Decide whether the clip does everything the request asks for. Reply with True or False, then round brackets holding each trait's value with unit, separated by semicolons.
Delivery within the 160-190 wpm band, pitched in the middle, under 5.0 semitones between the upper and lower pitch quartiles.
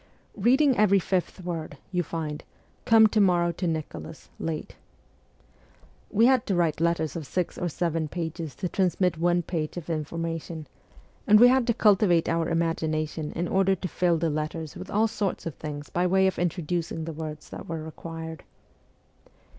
True (170 wpm; 170 Hz; 3.0 semitones)